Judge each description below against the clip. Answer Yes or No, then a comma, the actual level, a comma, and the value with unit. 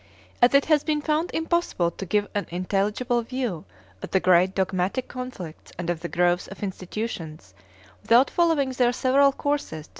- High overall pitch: Yes, high, 210 Hz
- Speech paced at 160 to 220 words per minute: Yes, average, 180 wpm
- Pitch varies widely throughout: Yes, wide, 7.0 semitones